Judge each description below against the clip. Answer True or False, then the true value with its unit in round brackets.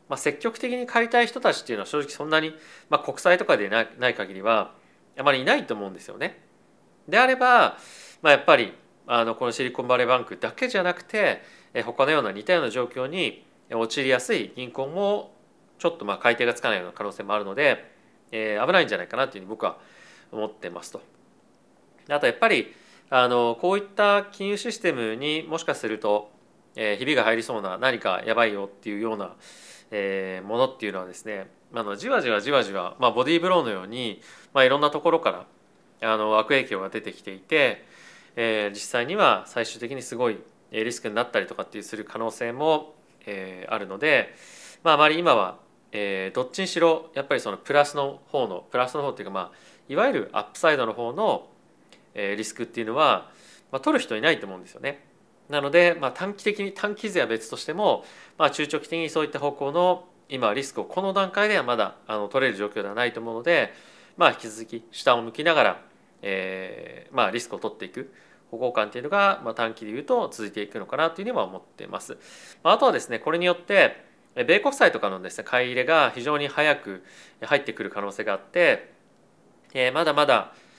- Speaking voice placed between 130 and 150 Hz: True (135 Hz)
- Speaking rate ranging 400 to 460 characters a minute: True (405 characters per minute)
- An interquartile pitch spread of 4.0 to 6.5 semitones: False (7.7 semitones)